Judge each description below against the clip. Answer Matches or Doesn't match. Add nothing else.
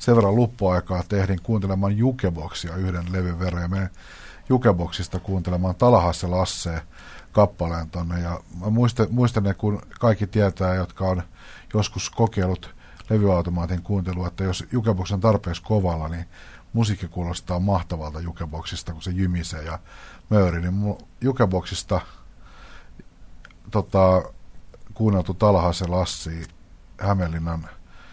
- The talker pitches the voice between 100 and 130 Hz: Doesn't match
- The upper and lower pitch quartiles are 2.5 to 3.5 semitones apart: Matches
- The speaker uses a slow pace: Doesn't match